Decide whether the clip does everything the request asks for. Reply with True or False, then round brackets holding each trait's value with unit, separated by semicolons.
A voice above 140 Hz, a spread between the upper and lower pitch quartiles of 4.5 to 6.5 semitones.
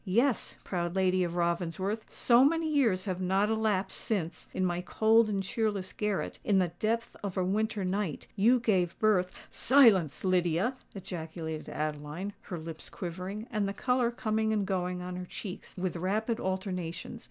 False (190 Hz; 3.4 semitones)